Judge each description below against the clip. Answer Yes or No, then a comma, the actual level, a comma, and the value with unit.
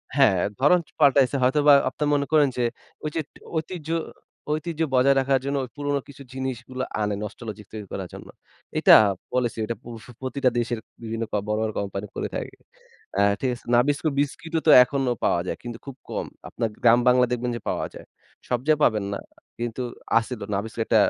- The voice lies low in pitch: Yes, low, 125 Hz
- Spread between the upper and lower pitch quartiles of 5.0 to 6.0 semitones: No, average, 3.8 semitones